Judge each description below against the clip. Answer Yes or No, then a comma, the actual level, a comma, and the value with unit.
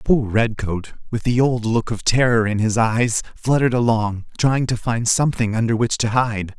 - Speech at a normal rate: Yes, average, 190 wpm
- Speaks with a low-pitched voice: Yes, low, 115 Hz